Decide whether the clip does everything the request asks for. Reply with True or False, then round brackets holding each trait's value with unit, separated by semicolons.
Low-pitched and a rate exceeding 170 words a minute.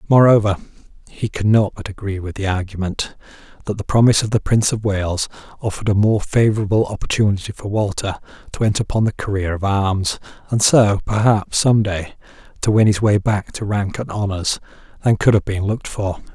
True (105 Hz; 185 wpm)